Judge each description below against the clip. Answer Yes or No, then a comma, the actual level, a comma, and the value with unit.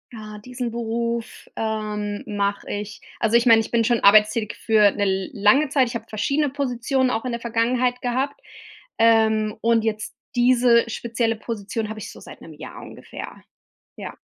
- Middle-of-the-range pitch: No, high, 230 Hz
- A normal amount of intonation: No, narrow, 2.3 semitones